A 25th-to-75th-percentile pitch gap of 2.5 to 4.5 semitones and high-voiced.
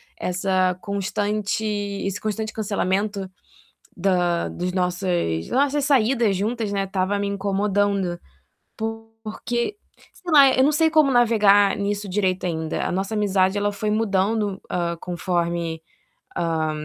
Yes: average, 3.0 semitones; high, 200 Hz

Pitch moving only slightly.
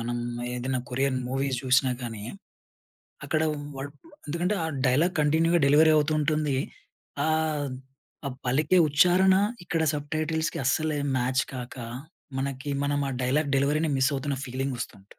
No: average, 3.1 semitones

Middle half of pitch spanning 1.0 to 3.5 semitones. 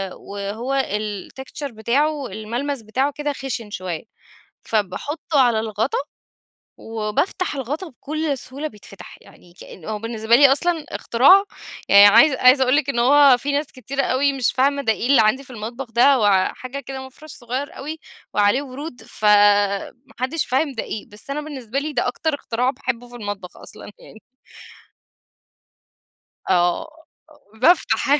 No: average, 4.6 semitones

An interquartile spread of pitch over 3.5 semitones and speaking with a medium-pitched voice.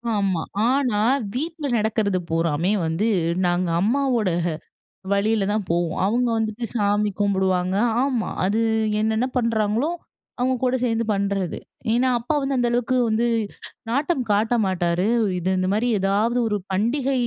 No: average, 4.2 semitones; high, 215 Hz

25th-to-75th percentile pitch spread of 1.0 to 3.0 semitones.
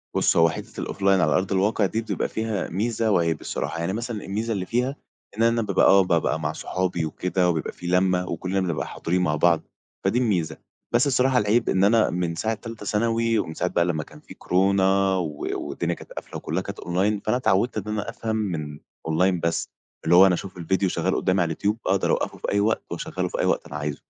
No: average, 3.9 semitones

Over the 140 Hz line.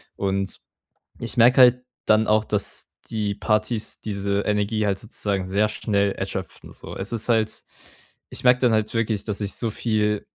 No: low, 105 Hz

